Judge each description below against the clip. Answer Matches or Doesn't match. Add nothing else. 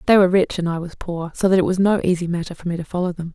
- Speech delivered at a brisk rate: Matches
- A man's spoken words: Doesn't match